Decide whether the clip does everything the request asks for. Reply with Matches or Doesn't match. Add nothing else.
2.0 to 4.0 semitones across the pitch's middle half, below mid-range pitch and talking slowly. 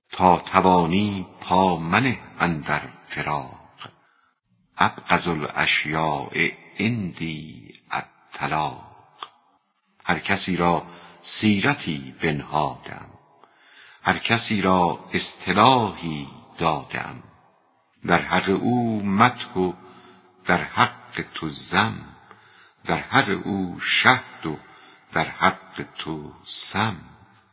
Matches